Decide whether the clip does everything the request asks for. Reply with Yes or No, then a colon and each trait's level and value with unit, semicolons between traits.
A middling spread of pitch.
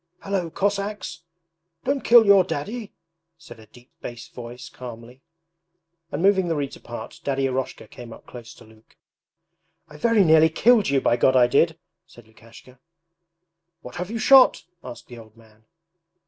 No: wide, 8.5 semitones